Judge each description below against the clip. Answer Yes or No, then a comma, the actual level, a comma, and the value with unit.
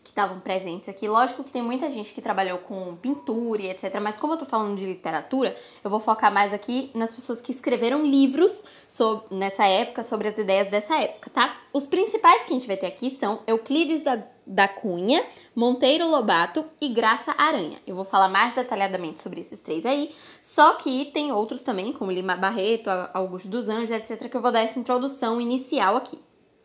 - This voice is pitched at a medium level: No, high, 230 Hz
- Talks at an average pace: No, fast, 195 wpm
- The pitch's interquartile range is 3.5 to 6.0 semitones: Yes, average, 5.2 semitones